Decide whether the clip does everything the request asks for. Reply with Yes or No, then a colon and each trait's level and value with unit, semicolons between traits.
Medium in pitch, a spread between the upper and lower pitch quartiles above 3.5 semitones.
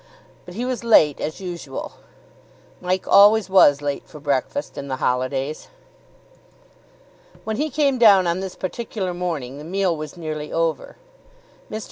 Yes: medium, 175 Hz; wide, 5.4 semitones